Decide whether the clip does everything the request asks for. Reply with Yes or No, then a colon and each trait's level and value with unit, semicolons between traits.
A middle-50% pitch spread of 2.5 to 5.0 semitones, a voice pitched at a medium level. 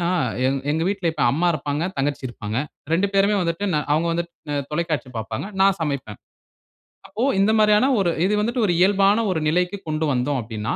No: wide, 5.5 semitones; medium, 170 Hz